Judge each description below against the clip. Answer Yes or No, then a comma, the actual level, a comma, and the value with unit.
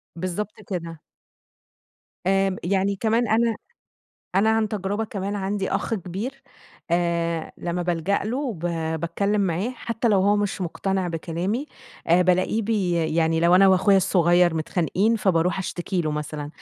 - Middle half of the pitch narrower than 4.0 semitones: Yes, average, 3.4 semitones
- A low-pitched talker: No, high, 190 Hz